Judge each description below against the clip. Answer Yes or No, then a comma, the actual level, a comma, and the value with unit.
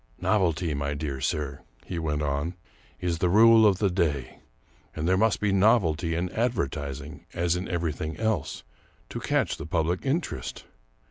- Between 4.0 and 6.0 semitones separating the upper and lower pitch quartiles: Yes, average, 4.7 semitones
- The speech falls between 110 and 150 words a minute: No, average, 175 wpm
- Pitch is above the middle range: No, very low, 85 Hz